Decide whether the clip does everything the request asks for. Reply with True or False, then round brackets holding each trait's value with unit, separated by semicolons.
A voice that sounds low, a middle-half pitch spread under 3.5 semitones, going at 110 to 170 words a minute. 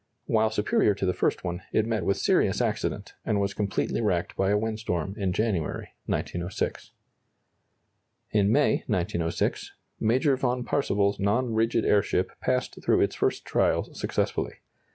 True (105 Hz; 2.6 semitones; 145 wpm)